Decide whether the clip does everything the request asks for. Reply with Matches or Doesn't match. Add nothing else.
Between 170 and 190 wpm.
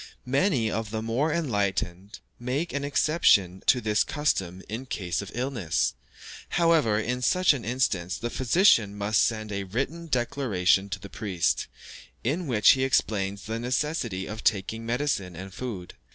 Doesn't match